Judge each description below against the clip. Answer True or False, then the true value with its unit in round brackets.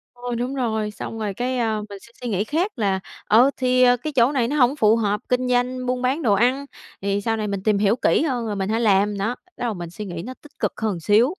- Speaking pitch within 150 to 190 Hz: False (230 Hz)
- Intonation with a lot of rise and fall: False (3.5 semitones)